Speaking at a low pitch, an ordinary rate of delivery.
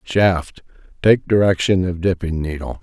No: very low, 90 Hz; slow, 125 wpm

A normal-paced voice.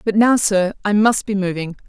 No: fast, 225 wpm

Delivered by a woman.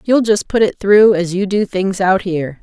Yes: female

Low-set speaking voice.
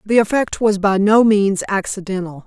No: high, 200 Hz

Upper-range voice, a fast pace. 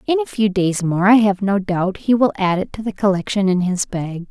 Yes: high, 200 Hz; fast, 265 wpm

